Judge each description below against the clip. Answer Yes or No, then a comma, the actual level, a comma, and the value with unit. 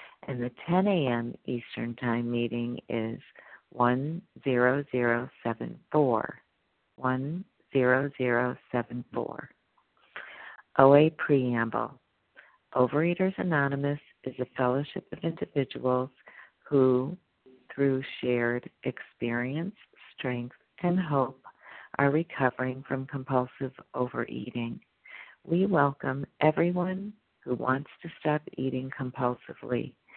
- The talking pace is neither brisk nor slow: No, slow, 80 wpm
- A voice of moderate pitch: No, low, 130 Hz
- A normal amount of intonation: Yes, average, 3.4 semitones